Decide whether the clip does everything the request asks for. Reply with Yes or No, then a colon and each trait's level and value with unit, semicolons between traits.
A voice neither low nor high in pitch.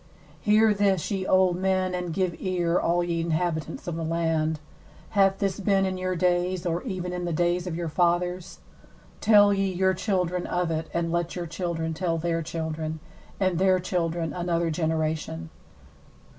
Yes: medium, 175 Hz